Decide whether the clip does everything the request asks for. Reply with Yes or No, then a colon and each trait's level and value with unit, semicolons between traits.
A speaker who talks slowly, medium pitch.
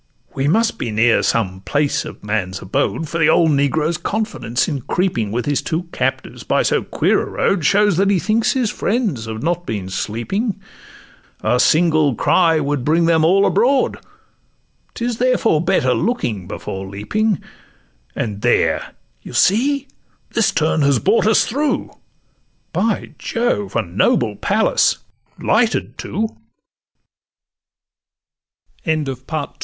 Yes: slow, 130 wpm; medium, 155 Hz